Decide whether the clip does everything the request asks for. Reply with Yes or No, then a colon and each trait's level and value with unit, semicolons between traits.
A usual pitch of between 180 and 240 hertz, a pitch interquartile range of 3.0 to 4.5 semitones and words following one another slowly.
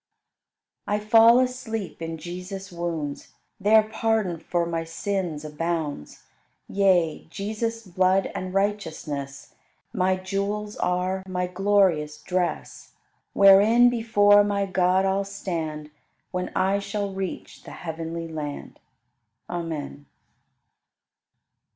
Yes: medium, 185 Hz; average, 3.5 semitones; slow, 105 wpm